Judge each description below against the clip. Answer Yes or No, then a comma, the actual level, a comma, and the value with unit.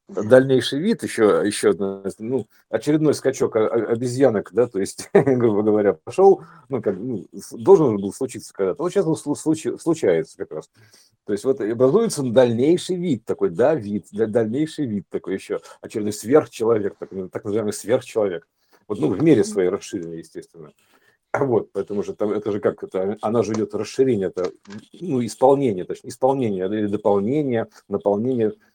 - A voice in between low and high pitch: No, low, 125 Hz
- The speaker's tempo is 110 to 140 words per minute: No, average, 155 wpm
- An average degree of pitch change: No, wide, 5.8 semitones